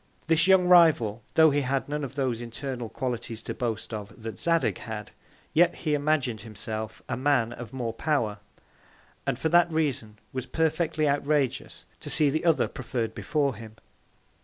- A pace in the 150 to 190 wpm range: Yes, average, 165 wpm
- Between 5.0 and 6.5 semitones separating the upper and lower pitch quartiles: Yes, average, 5.3 semitones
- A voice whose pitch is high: No, low, 135 Hz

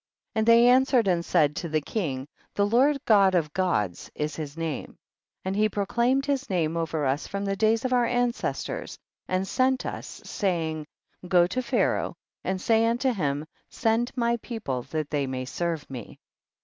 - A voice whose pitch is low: No, high, 190 Hz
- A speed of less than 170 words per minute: No, average, 175 wpm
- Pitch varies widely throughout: Yes, wide, 7.1 semitones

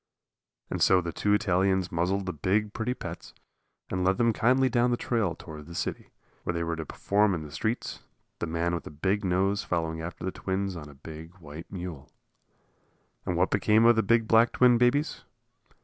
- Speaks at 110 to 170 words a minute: No, average, 195 wpm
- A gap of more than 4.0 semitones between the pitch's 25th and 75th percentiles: Yes, average, 4.6 semitones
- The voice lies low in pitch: Yes, very low, 95 Hz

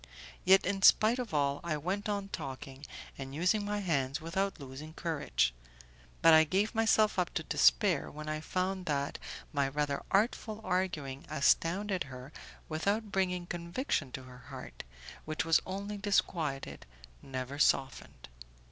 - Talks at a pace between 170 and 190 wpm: No, average, 145 wpm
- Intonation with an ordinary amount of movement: No, wide, 5.7 semitones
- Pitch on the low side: No, medium, 165 Hz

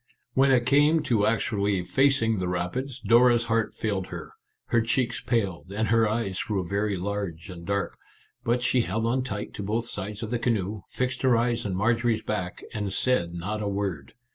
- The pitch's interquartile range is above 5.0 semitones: No, average, 3.3 semitones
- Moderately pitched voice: No, low, 110 Hz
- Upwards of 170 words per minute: Yes, average, 190 wpm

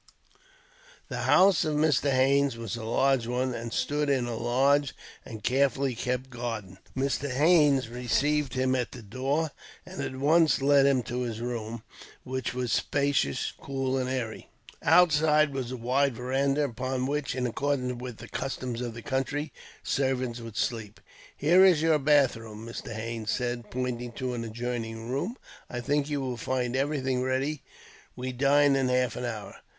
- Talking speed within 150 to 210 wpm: Yes, average, 165 wpm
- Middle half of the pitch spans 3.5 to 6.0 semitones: No, average, 2.8 semitones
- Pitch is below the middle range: Yes, low, 130 Hz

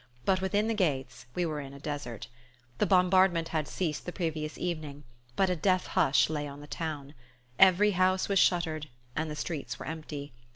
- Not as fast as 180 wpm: No, average, 190 wpm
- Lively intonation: No, average, 4.0 semitones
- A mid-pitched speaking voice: Yes, medium, 160 Hz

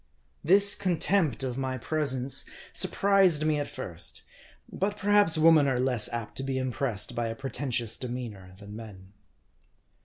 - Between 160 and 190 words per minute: No, average, 145 wpm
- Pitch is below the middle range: Yes, low, 130 Hz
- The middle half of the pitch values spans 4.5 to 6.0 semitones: Yes, average, 5.3 semitones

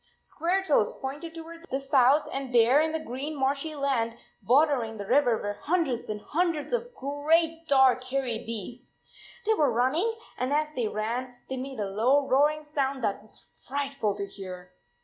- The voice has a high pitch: Yes, very high, 270 Hz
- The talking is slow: No, average, 170 wpm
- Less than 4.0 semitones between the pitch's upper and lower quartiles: No, average, 4.4 semitones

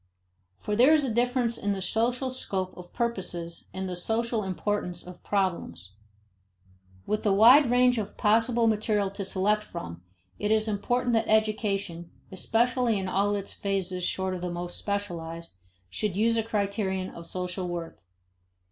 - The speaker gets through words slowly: No, average, 155 wpm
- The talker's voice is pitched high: Yes, high, 205 Hz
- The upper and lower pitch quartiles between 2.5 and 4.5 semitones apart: Yes, average, 3.6 semitones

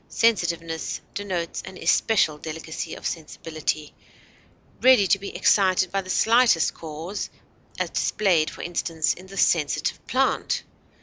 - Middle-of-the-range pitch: Yes, medium, 175 Hz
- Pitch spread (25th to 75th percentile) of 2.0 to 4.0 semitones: Yes, average, 3.5 semitones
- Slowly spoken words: Yes, slow, 125 wpm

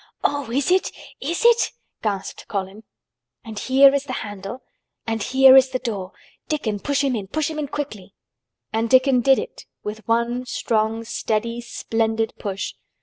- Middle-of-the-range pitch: No, high, 235 Hz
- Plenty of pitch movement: No, average, 4.0 semitones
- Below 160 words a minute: Yes, average, 150 wpm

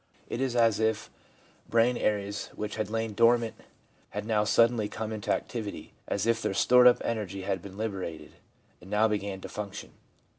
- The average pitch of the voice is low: Yes, low, 110 Hz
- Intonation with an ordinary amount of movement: No, narrow, 2.2 semitones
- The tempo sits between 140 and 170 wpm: No, average, 180 wpm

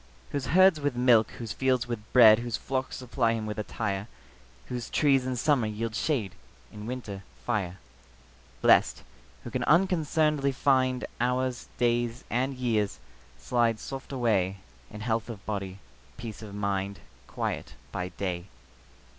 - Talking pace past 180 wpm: No, average, 140 wpm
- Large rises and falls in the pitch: No, average, 3.5 semitones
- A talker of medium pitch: No, low, 120 Hz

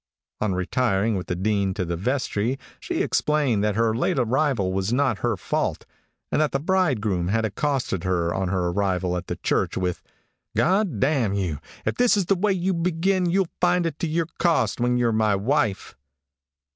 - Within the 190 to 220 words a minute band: Yes, average, 195 wpm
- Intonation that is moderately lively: No, wide, 8.1 semitones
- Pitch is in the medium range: No, low, 115 Hz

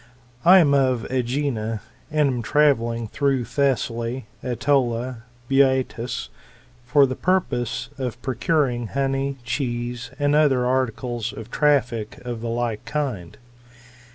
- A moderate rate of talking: No, slow, 120 wpm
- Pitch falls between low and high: No, low, 125 Hz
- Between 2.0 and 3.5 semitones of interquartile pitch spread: Yes, average, 2.9 semitones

